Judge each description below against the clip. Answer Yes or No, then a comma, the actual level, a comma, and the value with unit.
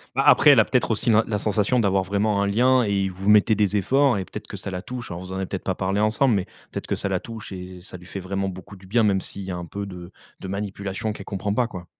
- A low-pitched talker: Yes, low, 100 Hz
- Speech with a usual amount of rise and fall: No, narrow, 2.2 semitones